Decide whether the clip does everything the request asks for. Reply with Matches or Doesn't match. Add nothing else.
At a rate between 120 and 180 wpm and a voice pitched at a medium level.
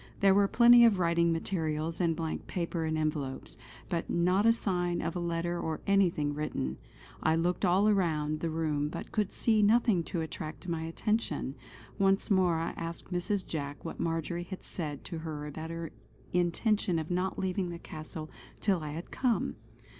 Matches